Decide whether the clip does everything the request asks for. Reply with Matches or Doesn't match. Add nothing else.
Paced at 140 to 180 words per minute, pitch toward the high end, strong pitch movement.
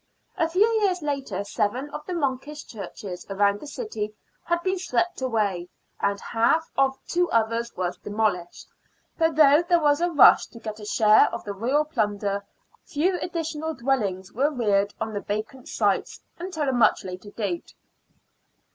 Matches